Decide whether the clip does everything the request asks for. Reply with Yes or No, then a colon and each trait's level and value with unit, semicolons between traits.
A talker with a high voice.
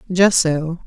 No: medium, 170 Hz